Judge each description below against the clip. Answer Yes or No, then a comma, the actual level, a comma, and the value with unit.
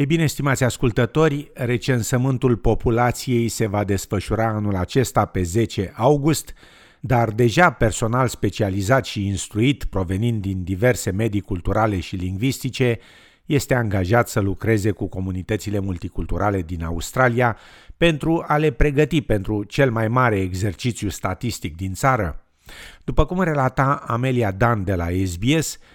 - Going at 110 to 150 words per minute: Yes, average, 130 wpm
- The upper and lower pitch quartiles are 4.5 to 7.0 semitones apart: Yes, average, 4.8 semitones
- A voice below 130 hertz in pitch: Yes, low, 115 Hz